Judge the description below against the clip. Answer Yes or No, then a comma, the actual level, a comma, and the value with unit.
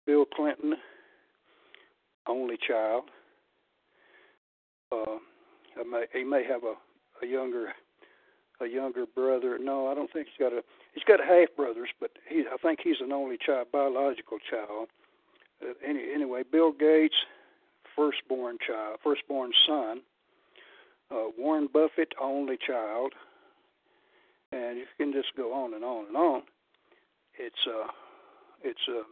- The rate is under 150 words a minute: Yes, slow, 135 wpm